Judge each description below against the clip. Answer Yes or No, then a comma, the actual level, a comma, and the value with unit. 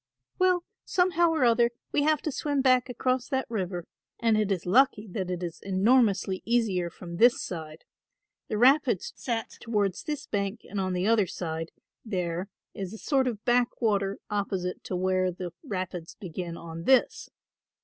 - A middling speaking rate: Yes, average, 165 wpm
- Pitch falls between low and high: No, high, 205 Hz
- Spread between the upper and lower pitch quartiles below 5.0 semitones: No, wide, 5.4 semitones